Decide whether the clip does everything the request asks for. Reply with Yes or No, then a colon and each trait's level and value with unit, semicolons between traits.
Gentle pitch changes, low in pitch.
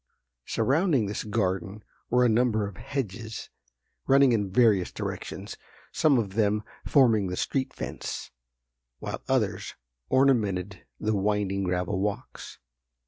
No: average, 4.1 semitones; low, 105 Hz